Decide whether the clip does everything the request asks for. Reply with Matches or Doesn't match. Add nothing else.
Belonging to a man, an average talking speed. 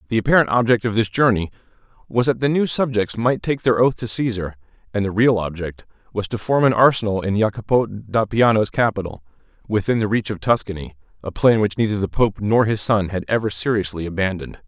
Matches